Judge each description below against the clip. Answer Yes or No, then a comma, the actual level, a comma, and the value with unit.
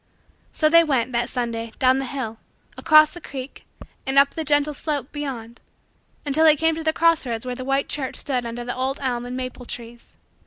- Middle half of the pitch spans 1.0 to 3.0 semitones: No, average, 3.6 semitones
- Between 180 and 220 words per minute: Yes, fast, 205 wpm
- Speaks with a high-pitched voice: Yes, very high, 265 Hz